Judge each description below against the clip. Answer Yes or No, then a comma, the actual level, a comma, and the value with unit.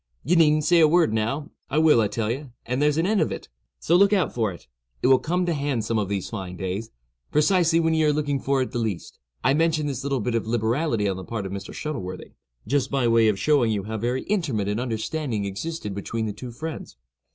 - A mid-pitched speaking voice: No, low, 125 Hz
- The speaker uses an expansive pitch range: Yes, wide, 6.1 semitones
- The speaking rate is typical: No, fast, 235 wpm